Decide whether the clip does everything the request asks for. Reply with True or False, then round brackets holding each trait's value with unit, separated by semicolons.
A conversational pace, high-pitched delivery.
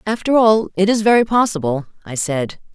True (175 wpm; 195 Hz)